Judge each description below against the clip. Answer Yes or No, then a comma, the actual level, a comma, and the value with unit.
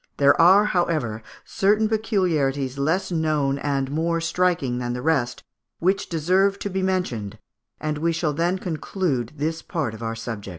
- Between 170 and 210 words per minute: No, average, 160 wpm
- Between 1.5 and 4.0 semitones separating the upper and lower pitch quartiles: No, average, 5.1 semitones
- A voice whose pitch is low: No, medium, 160 Hz